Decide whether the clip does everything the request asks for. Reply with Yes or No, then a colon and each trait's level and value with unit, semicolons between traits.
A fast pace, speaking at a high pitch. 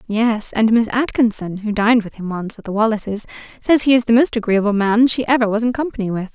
Yes: fast, 235 wpm; high, 225 Hz